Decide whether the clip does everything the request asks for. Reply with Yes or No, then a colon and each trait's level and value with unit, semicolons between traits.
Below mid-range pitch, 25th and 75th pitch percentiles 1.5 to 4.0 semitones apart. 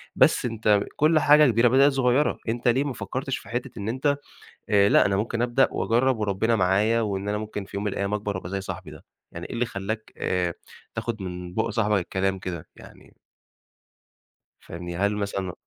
Yes: low, 105 Hz; average, 3.7 semitones